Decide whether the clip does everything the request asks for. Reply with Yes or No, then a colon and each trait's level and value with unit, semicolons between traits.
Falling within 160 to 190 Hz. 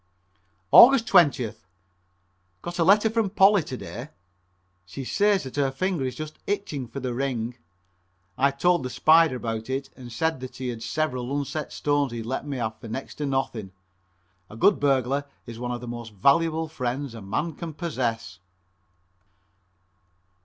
No: low, 135 Hz